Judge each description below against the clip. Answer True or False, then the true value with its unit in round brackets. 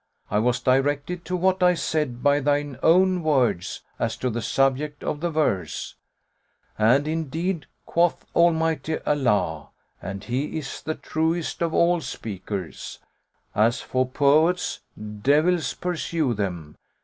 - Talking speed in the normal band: False (130 wpm)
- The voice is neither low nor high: True (145 Hz)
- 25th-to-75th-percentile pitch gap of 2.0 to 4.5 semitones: False (5.2 semitones)